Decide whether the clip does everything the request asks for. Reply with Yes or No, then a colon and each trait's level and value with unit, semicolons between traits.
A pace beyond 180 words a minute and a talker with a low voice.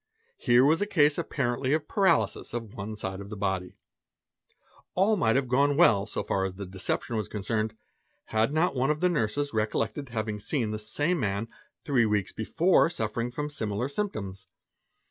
Yes: average, 195 wpm; low, 115 Hz